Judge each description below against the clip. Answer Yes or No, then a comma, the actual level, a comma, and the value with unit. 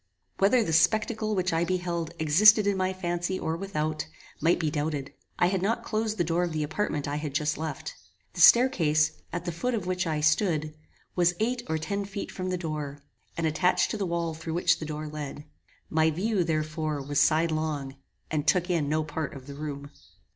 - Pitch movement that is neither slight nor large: Yes, average, 3.4 semitones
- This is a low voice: No, medium, 165 Hz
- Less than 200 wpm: No, fast, 205 wpm